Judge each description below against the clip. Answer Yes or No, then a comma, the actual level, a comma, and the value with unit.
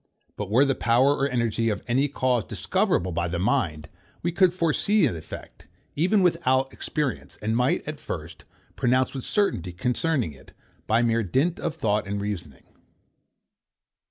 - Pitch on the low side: Yes, low, 125 Hz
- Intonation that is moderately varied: No, wide, 6.0 semitones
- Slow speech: No, average, 155 wpm